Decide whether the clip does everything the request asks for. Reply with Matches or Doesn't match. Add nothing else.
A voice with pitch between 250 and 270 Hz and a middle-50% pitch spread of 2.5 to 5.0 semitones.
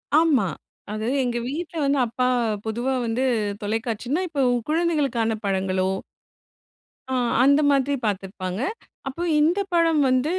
Doesn't match